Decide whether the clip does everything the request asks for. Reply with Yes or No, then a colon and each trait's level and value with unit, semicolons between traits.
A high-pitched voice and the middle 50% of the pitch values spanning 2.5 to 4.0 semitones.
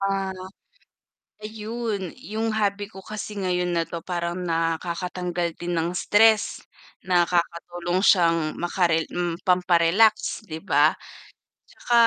No: medium, 180 Hz; average, 3.3 semitones